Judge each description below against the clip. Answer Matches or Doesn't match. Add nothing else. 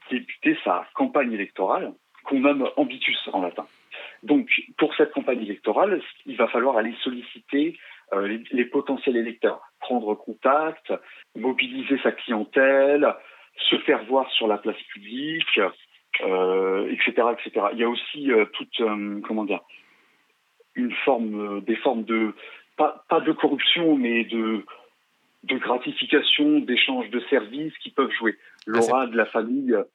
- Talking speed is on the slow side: Matches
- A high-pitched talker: Doesn't match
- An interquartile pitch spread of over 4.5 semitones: Matches